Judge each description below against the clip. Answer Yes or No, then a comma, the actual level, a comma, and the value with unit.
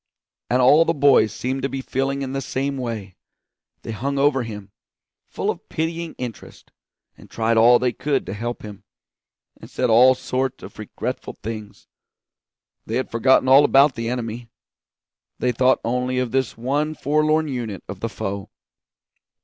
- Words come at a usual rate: Yes, average, 165 wpm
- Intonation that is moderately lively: Yes, average, 3.1 semitones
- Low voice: Yes, low, 125 Hz